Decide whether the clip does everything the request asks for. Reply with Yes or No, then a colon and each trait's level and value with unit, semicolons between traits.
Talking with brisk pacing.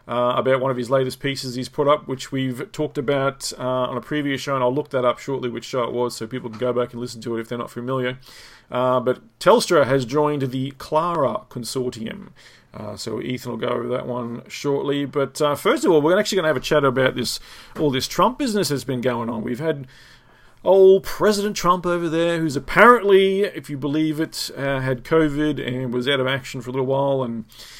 Yes: fast, 235 wpm